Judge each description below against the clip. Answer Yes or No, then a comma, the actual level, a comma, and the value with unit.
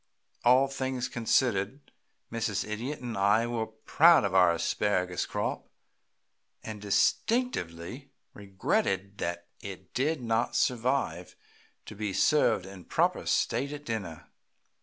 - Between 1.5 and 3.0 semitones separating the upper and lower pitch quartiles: No, average, 5.0 semitones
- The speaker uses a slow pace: Yes, slow, 115 wpm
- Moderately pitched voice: No, low, 110 Hz